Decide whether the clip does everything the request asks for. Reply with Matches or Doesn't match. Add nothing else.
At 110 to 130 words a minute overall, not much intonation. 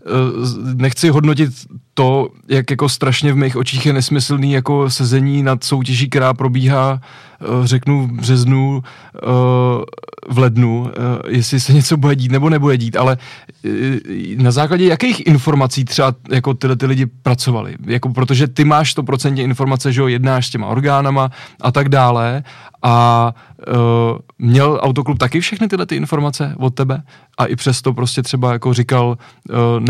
Doesn't match